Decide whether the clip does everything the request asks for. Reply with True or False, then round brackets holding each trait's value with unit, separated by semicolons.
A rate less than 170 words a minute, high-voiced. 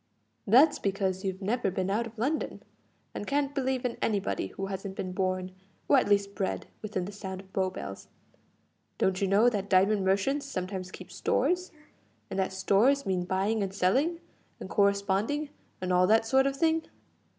False (175 wpm; 200 Hz)